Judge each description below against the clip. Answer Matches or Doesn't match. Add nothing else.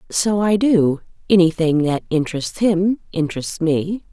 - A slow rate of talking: Matches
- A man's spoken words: Doesn't match